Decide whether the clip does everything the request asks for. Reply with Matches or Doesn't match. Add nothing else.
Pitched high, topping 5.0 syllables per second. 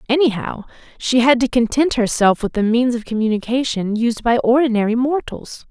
Matches